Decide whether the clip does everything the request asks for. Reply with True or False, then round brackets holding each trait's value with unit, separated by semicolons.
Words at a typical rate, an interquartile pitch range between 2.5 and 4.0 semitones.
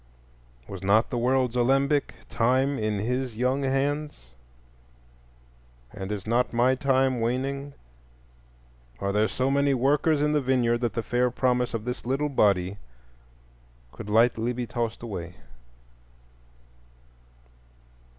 False (120 wpm; 3.0 semitones)